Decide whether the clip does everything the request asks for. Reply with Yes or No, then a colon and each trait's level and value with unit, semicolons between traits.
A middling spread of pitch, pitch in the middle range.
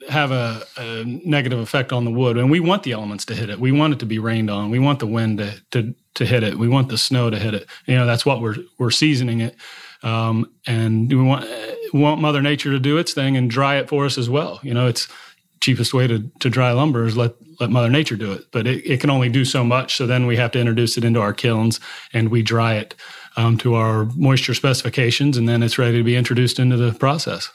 No: average, 3.0 semitones; low, 125 Hz